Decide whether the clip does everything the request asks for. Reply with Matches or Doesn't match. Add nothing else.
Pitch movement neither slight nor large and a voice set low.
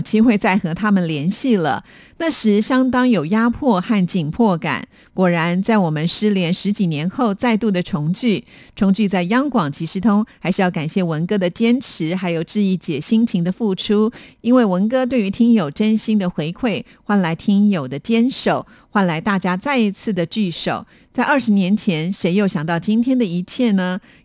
Doesn't match